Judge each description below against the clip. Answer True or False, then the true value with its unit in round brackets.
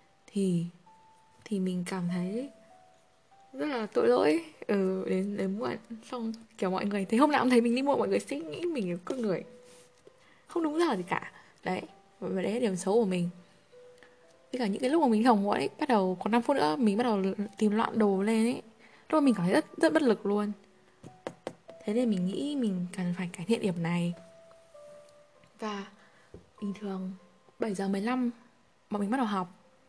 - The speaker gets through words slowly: False (205 wpm)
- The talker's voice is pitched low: False (210 Hz)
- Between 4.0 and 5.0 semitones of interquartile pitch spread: True (4.7 semitones)